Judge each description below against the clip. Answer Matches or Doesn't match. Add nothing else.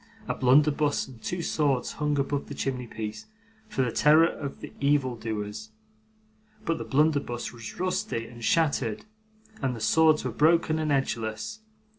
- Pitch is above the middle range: Doesn't match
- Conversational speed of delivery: Matches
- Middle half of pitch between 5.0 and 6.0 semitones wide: Doesn't match